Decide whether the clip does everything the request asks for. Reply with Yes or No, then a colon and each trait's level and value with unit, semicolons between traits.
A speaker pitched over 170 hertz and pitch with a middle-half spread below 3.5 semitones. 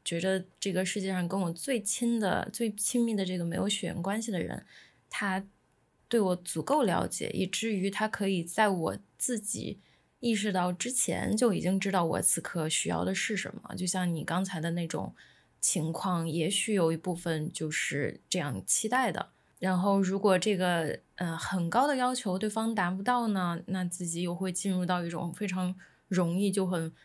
Yes: medium, 185 Hz; average, 2.9 semitones